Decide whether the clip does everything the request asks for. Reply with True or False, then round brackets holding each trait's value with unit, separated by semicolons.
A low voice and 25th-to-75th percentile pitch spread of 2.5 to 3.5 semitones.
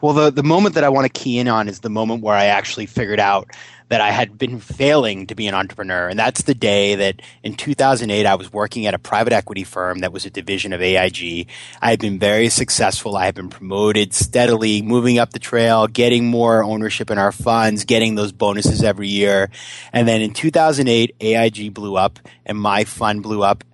True (110 Hz; 3.0 semitones)